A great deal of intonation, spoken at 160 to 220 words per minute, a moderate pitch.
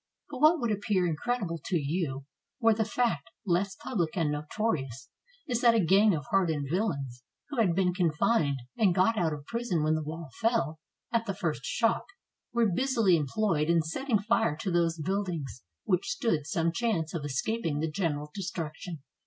Yes: wide, 6.3 semitones; average, 180 wpm; medium, 175 Hz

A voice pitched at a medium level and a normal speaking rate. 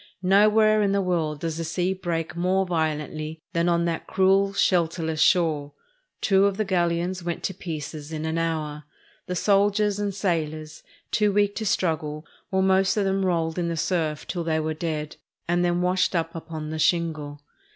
Yes: medium, 170 Hz; average, 180 wpm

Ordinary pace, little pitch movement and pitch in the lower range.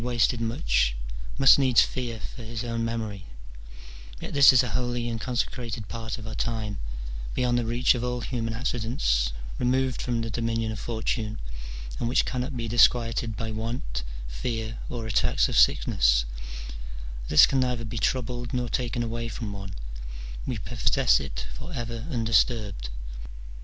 Yes: average, 155 wpm; narrow, 2.0 semitones; low, 115 Hz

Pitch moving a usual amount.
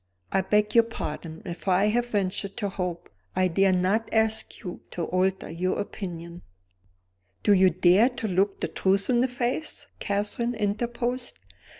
Yes: average, 3.8 semitones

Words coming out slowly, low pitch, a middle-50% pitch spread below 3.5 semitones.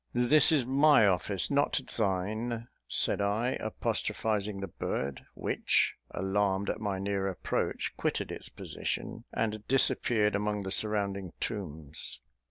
Yes: slow, 125 wpm; low, 105 Hz; narrow, 2.5 semitones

